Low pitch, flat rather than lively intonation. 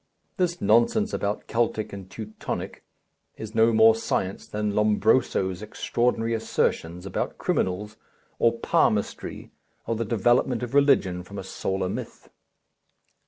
No: low, 110 Hz; average, 3.0 semitones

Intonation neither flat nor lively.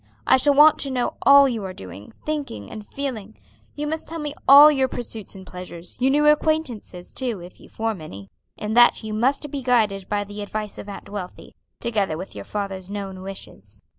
No: wide, 6.1 semitones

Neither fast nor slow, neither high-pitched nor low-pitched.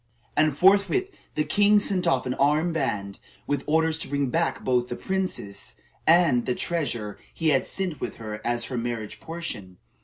Yes: average, 175 wpm; medium, 145 Hz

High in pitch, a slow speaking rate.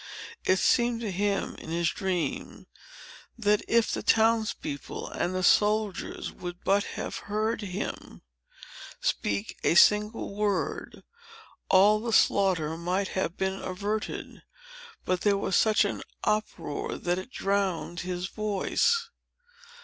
Yes: high, 200 Hz; slow, 125 wpm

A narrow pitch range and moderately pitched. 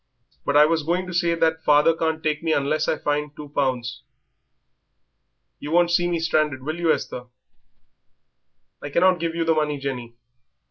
Yes: narrow, 2.3 semitones; medium, 155 Hz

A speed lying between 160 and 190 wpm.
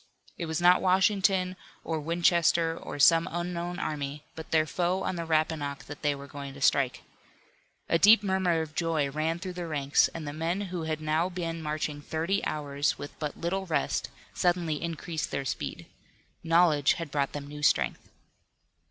Yes: average, 175 wpm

